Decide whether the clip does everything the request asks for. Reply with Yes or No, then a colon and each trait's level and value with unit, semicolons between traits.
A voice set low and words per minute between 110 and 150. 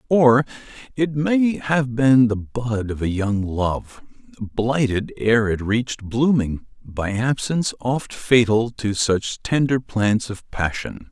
Yes: low, 120 Hz; slow, 135 wpm